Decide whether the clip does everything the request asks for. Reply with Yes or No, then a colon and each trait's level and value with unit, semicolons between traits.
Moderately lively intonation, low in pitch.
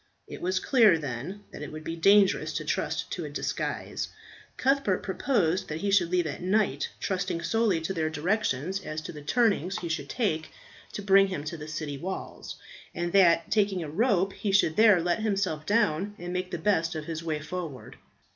No: average, 4.0 semitones; medium, 180 Hz